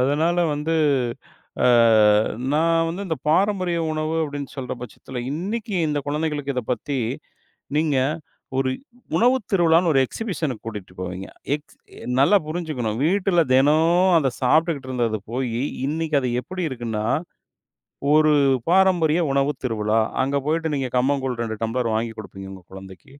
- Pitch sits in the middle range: Yes, medium, 145 Hz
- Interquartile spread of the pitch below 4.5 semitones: No, average, 5.0 semitones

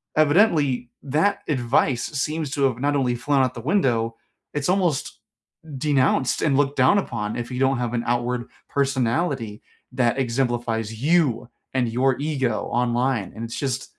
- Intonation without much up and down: No, average, 3.1 semitones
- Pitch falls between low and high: No, low, 130 Hz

